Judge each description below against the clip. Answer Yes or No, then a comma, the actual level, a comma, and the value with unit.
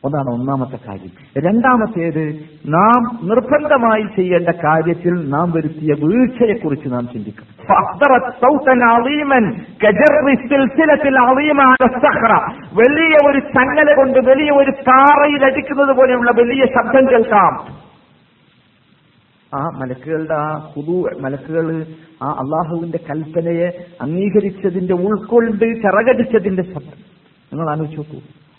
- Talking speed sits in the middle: Yes, average, 85 wpm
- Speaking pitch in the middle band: No, high, 205 Hz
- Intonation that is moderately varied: No, wide, 8.4 semitones